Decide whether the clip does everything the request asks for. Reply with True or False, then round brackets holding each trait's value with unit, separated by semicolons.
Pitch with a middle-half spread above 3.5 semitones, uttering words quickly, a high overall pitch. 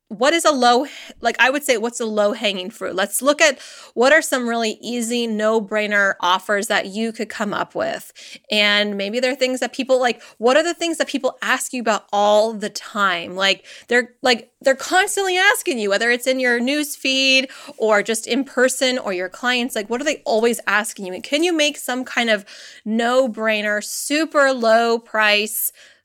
False (4.1 semitones; 195 wpm; 240 Hz)